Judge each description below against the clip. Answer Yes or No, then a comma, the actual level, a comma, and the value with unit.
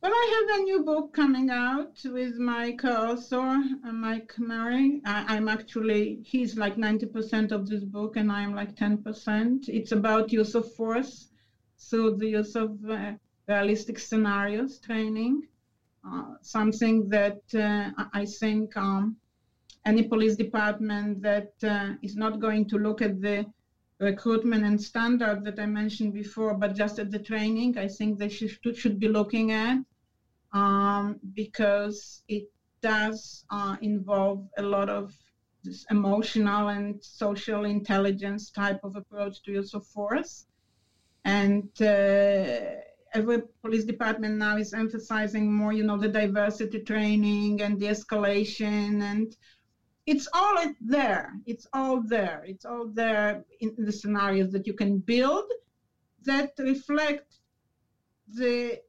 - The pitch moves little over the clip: Yes, narrow, 1.9 semitones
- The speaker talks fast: No, average, 140 wpm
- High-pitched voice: Yes, high, 215 Hz